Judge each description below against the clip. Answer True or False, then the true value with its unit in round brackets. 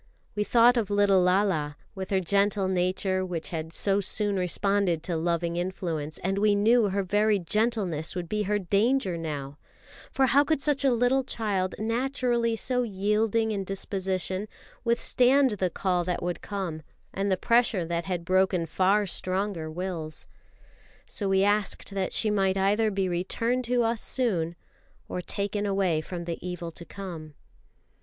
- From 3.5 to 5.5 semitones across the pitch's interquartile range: False (3.1 semitones)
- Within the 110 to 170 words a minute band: True (160 wpm)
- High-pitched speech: True (195 Hz)